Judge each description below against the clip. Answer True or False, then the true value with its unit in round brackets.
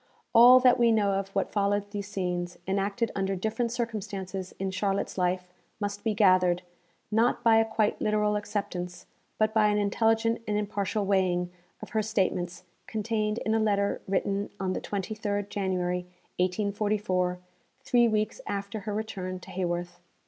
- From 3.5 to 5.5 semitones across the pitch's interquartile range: False (2.6 semitones)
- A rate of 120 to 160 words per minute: True (155 wpm)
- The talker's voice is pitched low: False (200 Hz)